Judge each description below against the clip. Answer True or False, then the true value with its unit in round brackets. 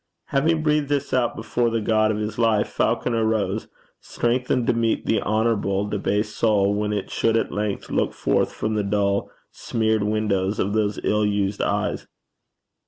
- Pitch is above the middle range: False (110 Hz)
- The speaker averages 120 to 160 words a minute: False (170 wpm)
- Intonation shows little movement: True (1.9 semitones)